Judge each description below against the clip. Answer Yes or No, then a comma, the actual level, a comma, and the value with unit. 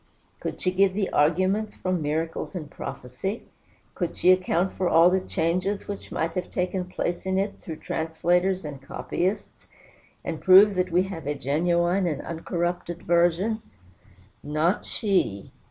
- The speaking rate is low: No, average, 150 wpm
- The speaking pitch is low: No, medium, 180 Hz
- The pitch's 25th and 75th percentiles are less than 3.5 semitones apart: Yes, narrow, 2.6 semitones